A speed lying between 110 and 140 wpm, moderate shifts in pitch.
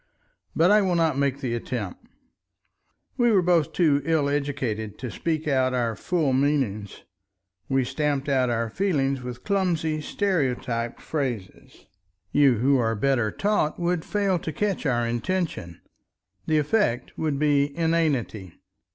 Yes: slow, 135 wpm; average, 5.0 semitones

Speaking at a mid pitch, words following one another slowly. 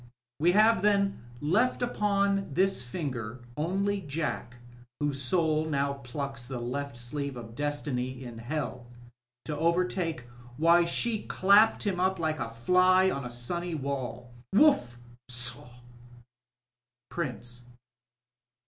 Yes: medium, 150 Hz; slow, 120 wpm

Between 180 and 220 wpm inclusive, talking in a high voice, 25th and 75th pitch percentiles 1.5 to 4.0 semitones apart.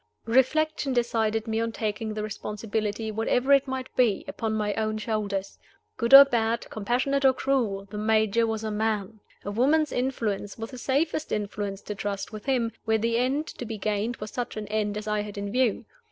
Yes: average, 195 wpm; high, 220 Hz; average, 2.9 semitones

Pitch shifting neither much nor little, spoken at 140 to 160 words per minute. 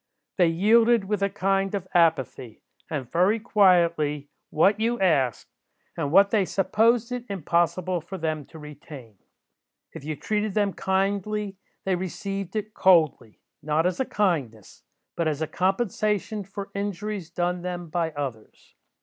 Yes: average, 4.3 semitones; average, 145 wpm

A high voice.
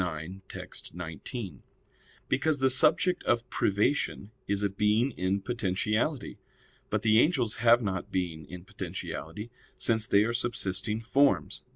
No: low, 110 Hz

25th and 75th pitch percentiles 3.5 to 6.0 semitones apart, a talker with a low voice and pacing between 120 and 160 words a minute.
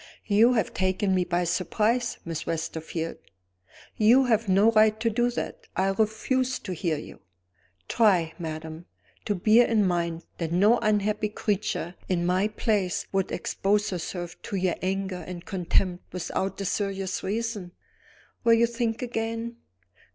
No: average, 3.9 semitones; high, 195 Hz; average, 145 wpm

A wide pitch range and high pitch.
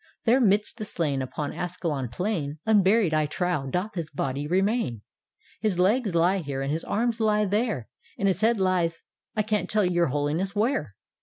No: wide, 6.0 semitones; medium, 180 Hz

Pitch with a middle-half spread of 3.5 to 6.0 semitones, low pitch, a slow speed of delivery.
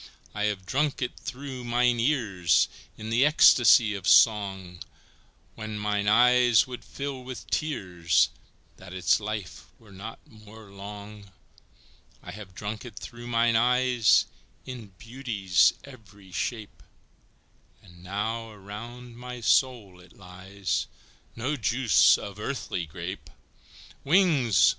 Yes: average, 3.9 semitones; low, 110 Hz; slow, 120 wpm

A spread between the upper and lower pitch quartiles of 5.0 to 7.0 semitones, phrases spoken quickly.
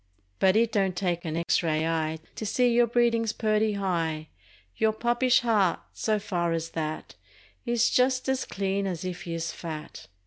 No: wide, 5.6 semitones; average, 170 wpm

